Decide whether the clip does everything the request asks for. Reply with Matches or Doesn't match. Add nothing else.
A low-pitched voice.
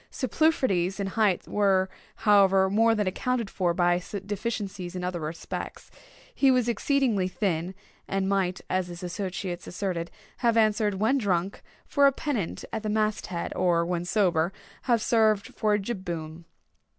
Doesn't match